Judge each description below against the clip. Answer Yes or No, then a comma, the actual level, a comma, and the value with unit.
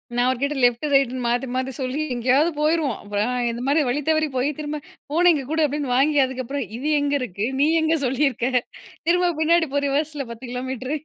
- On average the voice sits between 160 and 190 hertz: No, very high, 275 Hz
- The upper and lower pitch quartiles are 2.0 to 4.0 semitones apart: Yes, average, 3.3 semitones